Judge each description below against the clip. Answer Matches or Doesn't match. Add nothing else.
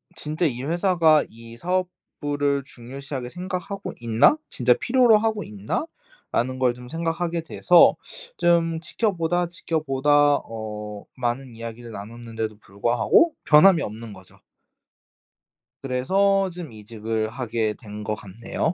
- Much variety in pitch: Matches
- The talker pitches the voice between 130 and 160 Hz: Matches